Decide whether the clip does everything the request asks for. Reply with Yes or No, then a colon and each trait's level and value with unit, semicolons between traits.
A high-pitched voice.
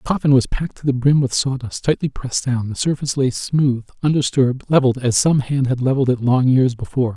No: low, 130 Hz